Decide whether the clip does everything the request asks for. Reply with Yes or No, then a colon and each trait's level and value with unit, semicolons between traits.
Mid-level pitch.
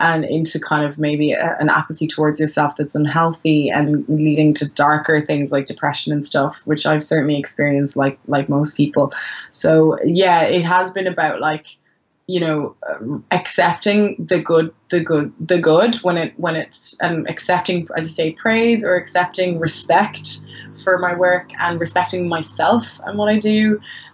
Yes: medium, 160 Hz